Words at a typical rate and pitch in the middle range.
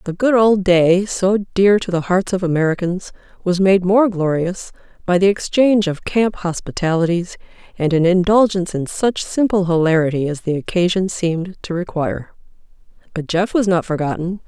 Yes: average, 160 wpm; medium, 180 Hz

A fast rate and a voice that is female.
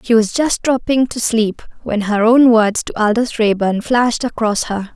No: average, 195 wpm; female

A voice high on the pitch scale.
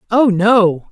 Yes: high, 205 Hz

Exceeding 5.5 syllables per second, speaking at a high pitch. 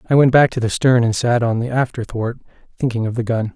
No: 5.9 syllables/s; low, 120 Hz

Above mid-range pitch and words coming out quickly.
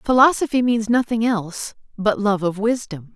No: high, 220 Hz; average, 150 wpm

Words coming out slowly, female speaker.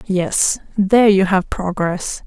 Yes: slow, 130 wpm; female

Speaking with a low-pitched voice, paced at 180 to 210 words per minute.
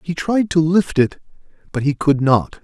No: medium, 155 Hz; fast, 205 wpm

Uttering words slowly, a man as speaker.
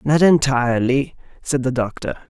Yes: slow, 125 wpm; male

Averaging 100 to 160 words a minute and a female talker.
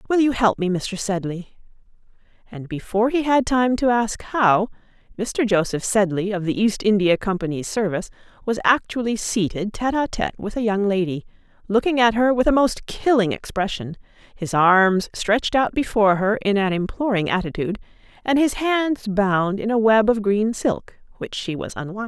No: average, 175 wpm; female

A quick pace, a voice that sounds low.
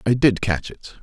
Yes: fast, 235 wpm; low, 110 Hz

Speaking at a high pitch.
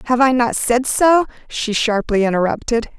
Yes: high, 240 Hz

